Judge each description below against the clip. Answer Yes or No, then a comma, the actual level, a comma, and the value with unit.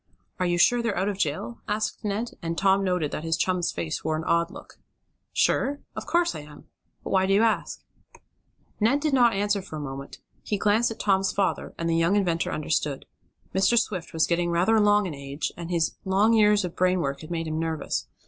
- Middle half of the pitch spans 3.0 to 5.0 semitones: Yes, average, 4.2 semitones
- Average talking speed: No, fast, 215 wpm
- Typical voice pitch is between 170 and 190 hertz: Yes, medium, 185 Hz